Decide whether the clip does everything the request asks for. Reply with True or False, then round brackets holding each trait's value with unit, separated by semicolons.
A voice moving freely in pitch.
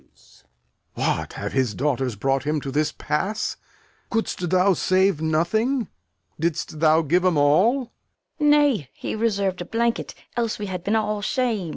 True (6.3 semitones)